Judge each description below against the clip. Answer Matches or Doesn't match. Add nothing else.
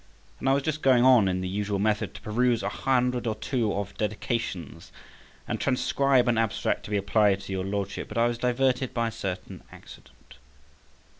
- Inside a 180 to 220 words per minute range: Matches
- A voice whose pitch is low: Matches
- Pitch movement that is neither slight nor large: Matches